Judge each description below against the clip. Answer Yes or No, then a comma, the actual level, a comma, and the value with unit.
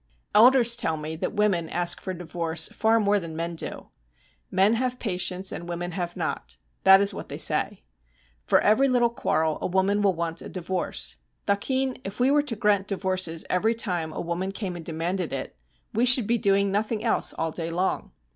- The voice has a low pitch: No, high, 190 Hz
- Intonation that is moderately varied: Yes, average, 4.2 semitones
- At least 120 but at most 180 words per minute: No, average, 195 wpm